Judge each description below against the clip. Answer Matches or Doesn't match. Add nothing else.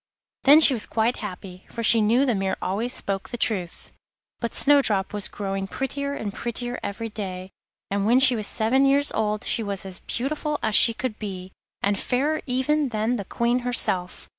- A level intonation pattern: Doesn't match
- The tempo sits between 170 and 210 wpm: Matches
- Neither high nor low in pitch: Doesn't match